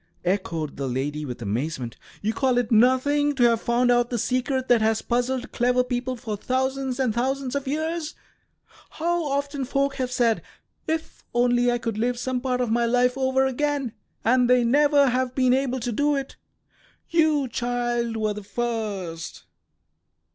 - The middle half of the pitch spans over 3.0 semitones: No, narrow, 2.6 semitones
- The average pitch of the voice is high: Yes, very high, 250 Hz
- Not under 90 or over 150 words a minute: No, average, 170 wpm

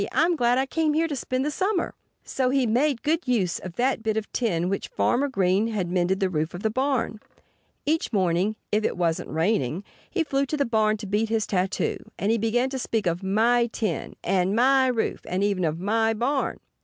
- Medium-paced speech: No, fast, 215 wpm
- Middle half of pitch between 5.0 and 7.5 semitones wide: Yes, wide, 5.6 semitones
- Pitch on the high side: Yes, high, 225 Hz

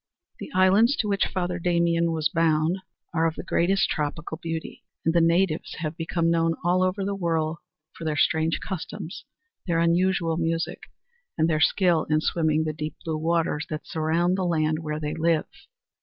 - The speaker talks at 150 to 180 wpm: Yes, average, 175 wpm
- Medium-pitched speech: Yes, medium, 165 Hz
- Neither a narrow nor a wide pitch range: No, narrow, 1.8 semitones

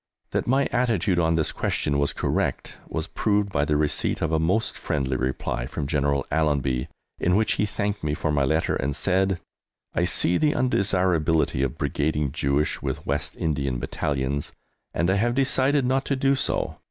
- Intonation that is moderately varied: No, wide, 6.1 semitones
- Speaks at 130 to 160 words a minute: No, average, 175 wpm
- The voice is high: No, very low, 80 Hz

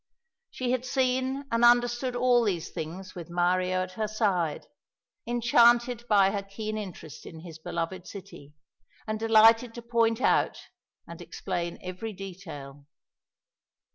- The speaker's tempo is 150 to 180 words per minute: No, slow, 135 wpm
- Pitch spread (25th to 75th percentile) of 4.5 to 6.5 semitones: Yes, average, 4.9 semitones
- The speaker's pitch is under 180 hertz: No, high, 215 Hz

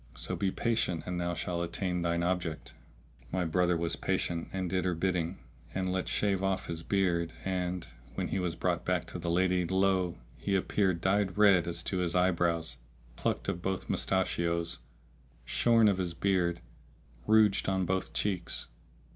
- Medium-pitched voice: No, very low, 90 Hz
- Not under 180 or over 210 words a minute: No, average, 165 wpm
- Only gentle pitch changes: Yes, narrow, 1.9 semitones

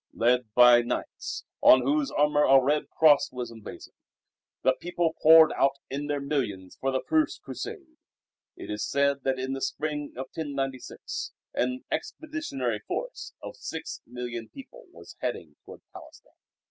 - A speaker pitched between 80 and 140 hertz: Yes, low, 135 Hz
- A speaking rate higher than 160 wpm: No, average, 150 wpm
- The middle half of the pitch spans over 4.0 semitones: No, average, 3.5 semitones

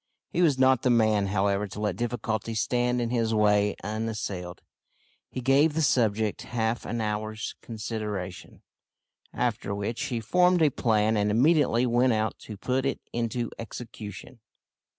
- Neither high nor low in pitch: No, low, 115 Hz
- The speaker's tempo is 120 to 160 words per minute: Yes, average, 150 wpm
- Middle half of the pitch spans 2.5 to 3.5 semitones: Yes, average, 2.8 semitones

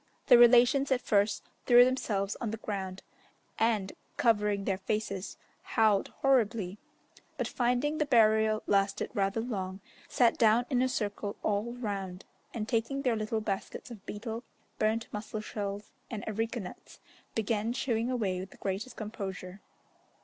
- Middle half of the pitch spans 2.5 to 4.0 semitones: Yes, average, 3.0 semitones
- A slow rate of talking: No, average, 145 wpm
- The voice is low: No, high, 215 Hz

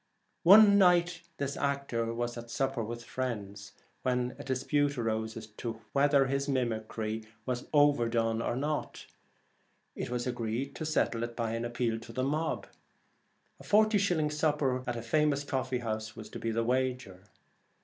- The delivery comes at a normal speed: Yes, average, 160 wpm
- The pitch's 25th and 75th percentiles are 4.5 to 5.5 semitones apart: No, average, 3.7 semitones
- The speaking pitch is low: Yes, low, 125 Hz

